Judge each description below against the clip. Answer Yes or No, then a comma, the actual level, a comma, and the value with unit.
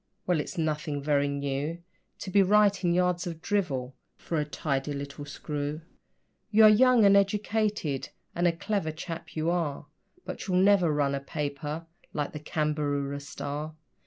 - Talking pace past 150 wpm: Yes, average, 160 wpm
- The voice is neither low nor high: Yes, medium, 155 Hz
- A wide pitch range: No, average, 4.2 semitones